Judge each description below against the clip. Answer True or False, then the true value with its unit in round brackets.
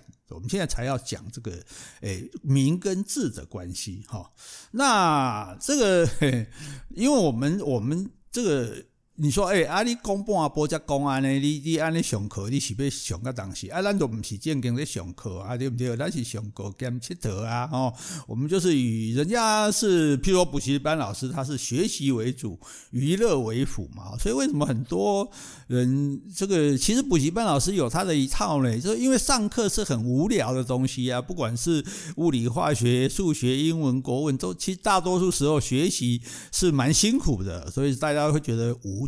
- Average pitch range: False (6.4 semitones)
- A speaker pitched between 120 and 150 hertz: True (140 Hz)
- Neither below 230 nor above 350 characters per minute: True (270 characters per minute)